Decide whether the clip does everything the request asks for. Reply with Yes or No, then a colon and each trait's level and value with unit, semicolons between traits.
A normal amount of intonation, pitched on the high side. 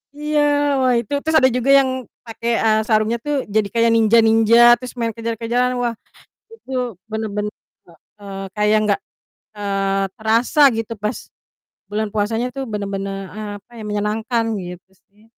No: narrow, 2.1 semitones; high, 220 Hz